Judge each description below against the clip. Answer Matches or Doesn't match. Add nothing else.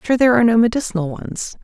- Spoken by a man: Doesn't match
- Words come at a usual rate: Doesn't match